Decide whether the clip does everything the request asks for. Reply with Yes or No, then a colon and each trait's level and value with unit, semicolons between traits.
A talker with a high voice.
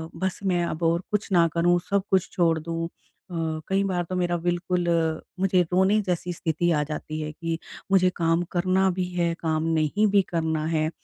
No: medium, 175 Hz